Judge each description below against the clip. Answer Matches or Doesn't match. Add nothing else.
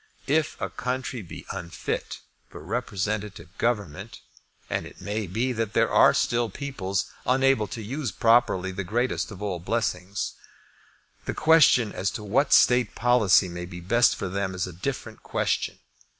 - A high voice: Doesn't match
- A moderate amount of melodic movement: Matches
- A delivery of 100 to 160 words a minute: Matches